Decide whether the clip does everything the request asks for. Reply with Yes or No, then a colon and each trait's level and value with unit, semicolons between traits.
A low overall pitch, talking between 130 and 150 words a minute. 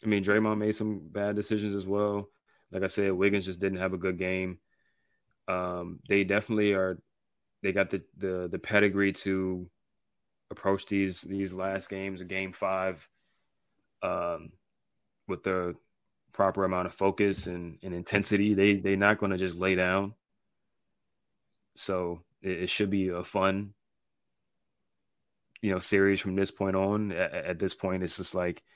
No: very low, 95 Hz; average, 160 wpm